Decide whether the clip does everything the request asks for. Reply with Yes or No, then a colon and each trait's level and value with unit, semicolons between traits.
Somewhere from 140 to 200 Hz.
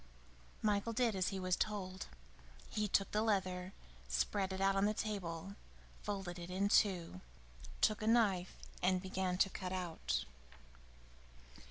Yes: high, 190 Hz